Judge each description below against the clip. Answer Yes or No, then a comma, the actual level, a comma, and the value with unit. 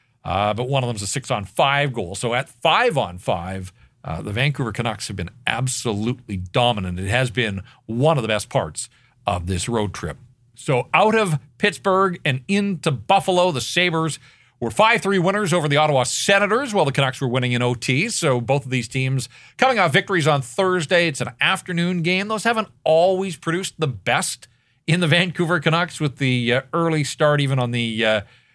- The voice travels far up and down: Yes, wide, 6.3 semitones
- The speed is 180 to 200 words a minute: Yes, average, 185 wpm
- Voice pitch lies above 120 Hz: Yes, low, 135 Hz